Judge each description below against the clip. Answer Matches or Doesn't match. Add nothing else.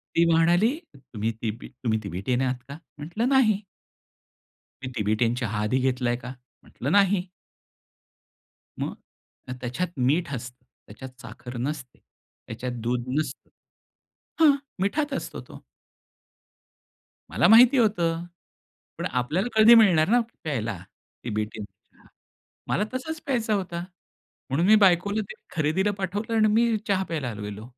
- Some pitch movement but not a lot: Doesn't match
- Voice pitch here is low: Doesn't match